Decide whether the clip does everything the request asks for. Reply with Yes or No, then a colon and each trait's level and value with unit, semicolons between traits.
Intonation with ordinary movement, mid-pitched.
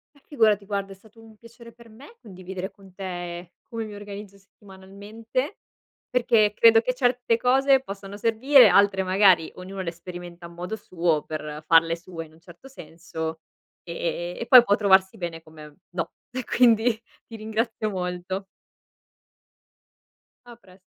No: average, 4.3 semitones; high, 195 Hz